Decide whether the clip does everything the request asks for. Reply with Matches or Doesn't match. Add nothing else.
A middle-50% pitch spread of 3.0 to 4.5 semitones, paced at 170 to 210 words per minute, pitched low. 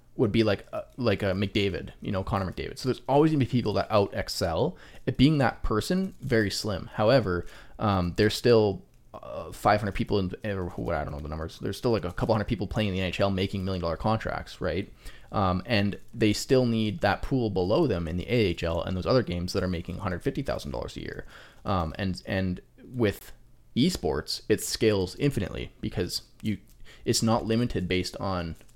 Matches